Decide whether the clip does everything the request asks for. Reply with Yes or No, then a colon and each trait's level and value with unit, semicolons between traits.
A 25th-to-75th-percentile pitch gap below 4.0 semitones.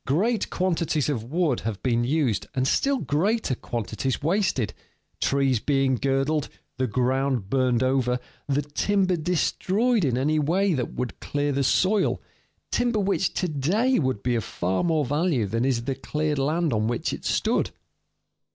No: wide, 5.5 semitones